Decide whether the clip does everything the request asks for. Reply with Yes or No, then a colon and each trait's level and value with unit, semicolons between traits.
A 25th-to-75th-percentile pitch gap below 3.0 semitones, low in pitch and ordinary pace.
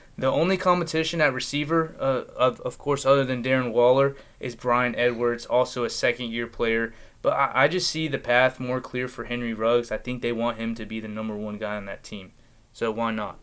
No: narrow, 2.5 semitones; low, 125 Hz; fast, 225 wpm